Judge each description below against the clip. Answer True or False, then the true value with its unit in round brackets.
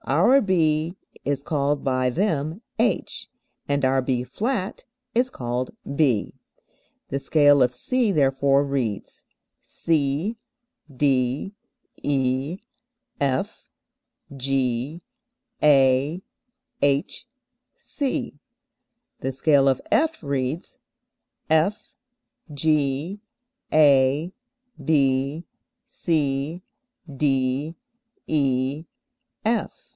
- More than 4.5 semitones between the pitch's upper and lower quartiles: False (3.4 semitones)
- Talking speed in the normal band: False (80 wpm)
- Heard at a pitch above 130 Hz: True (140 Hz)